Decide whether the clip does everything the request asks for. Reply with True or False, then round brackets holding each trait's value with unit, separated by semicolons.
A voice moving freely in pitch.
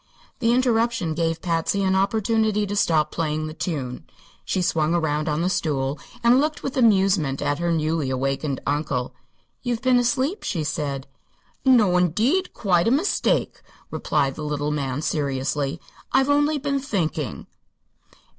True (7.5 semitones)